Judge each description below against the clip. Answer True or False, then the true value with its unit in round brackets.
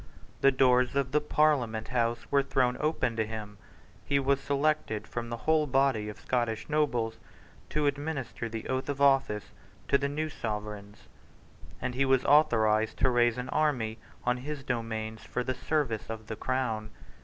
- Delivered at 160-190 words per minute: True (165 wpm)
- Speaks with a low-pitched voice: True (125 Hz)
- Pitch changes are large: False (3.8 semitones)